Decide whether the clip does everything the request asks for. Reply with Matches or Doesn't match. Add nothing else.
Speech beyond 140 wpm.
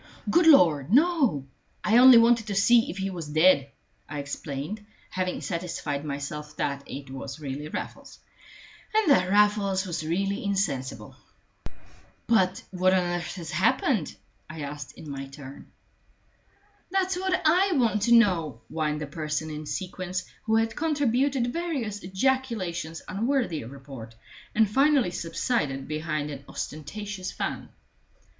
Doesn't match